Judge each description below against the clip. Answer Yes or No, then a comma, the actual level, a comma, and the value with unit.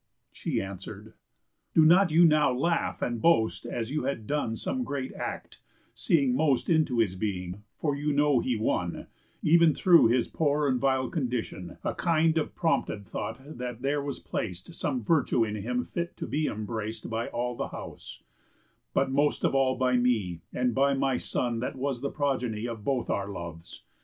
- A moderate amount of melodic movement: Yes, average, 4.7 semitones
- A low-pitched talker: Yes, low, 130 Hz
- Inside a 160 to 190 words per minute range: Yes, average, 180 wpm